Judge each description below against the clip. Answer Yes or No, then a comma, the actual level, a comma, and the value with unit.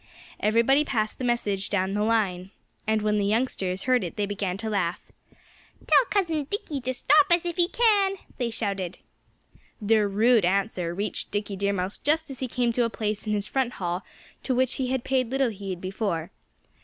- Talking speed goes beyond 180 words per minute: Yes, average, 190 wpm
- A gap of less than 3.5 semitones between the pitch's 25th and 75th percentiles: No, average, 4.6 semitones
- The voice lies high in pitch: Yes, high, 220 Hz